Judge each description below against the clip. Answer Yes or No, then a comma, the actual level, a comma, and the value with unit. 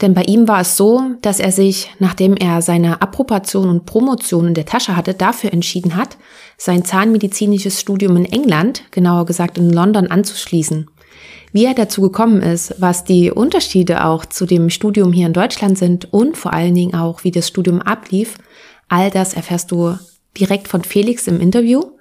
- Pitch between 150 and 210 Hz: Yes, high, 190 Hz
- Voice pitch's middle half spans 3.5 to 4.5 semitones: No, average, 3.0 semitones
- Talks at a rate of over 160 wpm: Yes, average, 180 wpm